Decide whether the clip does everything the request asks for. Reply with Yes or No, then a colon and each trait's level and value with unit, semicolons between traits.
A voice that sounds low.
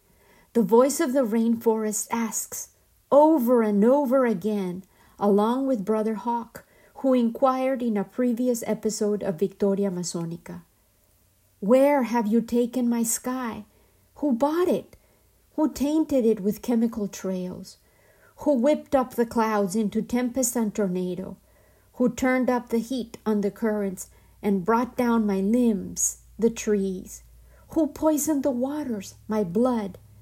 No: high, 230 Hz